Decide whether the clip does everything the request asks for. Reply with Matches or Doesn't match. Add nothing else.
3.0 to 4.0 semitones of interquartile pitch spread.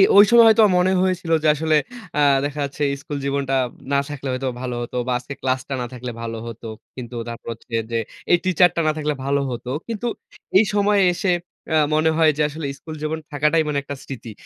Doesn't match